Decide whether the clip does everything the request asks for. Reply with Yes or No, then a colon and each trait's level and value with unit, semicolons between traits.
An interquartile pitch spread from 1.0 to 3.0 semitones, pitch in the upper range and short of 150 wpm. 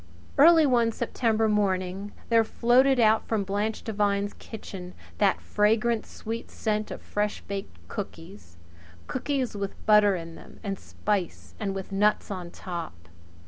Yes: narrow, 2.5 semitones; high, 210 Hz; average, 140 wpm